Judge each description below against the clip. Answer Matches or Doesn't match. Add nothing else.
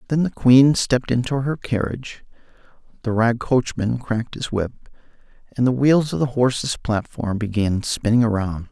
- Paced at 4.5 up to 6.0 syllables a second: Matches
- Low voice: Matches